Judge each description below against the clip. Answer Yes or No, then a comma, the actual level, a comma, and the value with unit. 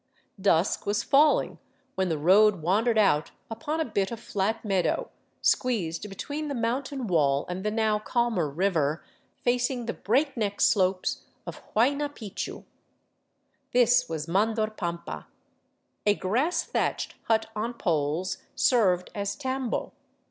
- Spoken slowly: Yes, slow, 130 wpm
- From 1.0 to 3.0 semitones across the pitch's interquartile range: No, average, 4.8 semitones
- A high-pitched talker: Yes, high, 210 Hz